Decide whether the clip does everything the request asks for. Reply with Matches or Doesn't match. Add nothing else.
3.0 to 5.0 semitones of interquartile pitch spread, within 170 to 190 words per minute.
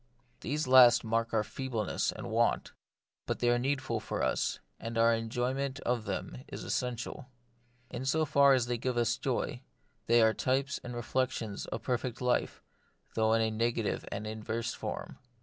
Doesn't match